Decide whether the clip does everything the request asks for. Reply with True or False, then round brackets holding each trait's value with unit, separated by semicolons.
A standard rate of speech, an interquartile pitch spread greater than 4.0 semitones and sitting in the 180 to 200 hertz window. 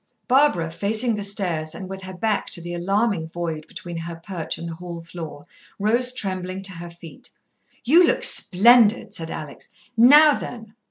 True (170 wpm; 4.9 semitones; 185 Hz)